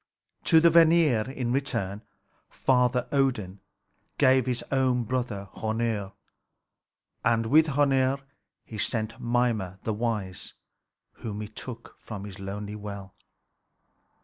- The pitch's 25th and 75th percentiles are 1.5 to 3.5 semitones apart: No, average, 4.1 semitones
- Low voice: Yes, low, 115 Hz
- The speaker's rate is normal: No, slow, 115 wpm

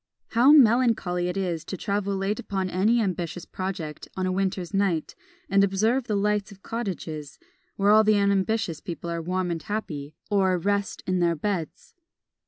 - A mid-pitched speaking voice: No, high, 195 Hz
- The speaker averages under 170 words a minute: No, average, 175 wpm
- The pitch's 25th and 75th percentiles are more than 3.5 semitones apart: No, average, 2.8 semitones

